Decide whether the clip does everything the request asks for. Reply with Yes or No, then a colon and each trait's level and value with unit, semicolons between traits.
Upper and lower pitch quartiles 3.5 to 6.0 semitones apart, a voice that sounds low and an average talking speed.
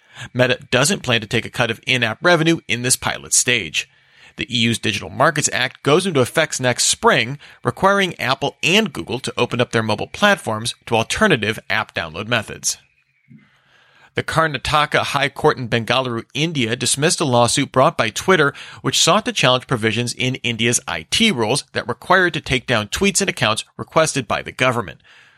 Yes: wide, 5.5 semitones; low, 125 Hz; average, 175 wpm